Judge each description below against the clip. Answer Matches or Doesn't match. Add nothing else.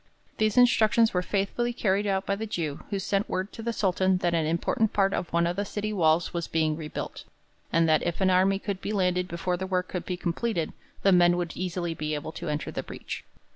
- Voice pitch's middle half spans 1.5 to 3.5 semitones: Matches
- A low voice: Doesn't match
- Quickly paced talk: Matches